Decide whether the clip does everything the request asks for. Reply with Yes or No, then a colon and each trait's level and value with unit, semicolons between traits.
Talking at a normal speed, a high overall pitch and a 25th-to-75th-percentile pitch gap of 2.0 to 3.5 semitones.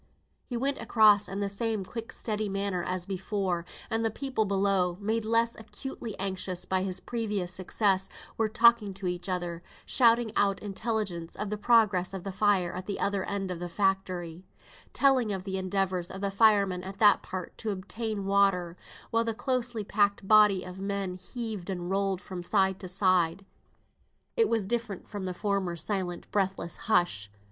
Yes: average, 175 wpm; high, 195 Hz; average, 2.7 semitones